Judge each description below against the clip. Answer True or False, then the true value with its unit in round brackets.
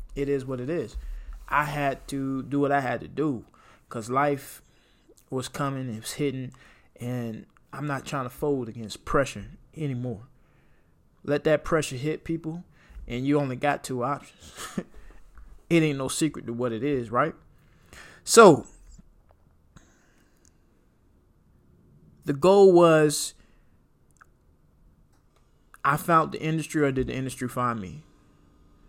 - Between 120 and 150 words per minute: True (135 wpm)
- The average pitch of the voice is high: False (135 Hz)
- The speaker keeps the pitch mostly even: False (3.3 semitones)